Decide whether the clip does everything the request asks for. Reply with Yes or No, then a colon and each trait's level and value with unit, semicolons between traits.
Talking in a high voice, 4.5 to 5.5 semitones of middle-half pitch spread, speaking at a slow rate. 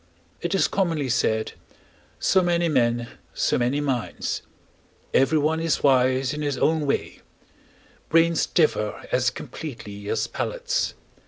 No: medium, 145 Hz; average, 4.9 semitones; slow, 120 wpm